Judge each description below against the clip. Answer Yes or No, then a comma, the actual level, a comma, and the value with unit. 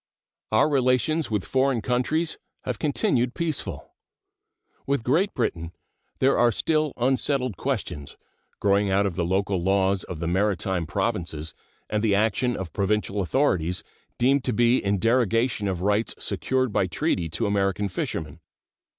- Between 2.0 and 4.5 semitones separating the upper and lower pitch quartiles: No, average, 5.2 semitones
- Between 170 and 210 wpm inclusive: No, average, 140 wpm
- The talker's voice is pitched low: Yes, low, 105 Hz